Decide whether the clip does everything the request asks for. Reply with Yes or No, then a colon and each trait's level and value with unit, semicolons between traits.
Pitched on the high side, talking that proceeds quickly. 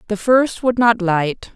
No: high, 215 Hz; average, 195 wpm